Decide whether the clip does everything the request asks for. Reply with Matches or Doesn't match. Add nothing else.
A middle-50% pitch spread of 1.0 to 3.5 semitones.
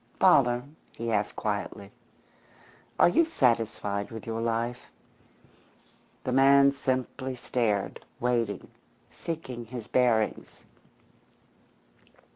Matches